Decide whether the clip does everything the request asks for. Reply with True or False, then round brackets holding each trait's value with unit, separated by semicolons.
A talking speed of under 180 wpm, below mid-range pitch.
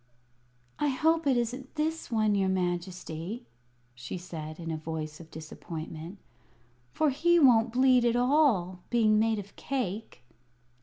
False (140 wpm; 215 Hz)